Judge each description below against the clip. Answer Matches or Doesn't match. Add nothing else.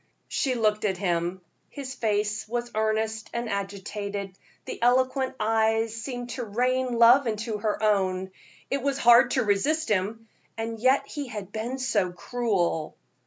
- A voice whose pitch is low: Doesn't match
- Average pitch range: Matches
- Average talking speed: Matches